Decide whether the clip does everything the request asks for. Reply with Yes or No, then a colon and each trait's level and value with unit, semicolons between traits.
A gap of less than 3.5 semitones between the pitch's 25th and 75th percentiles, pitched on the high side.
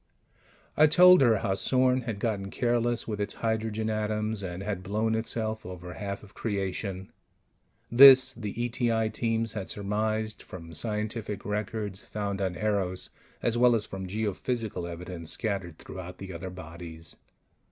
No: average, 3.1 semitones; low, 105 Hz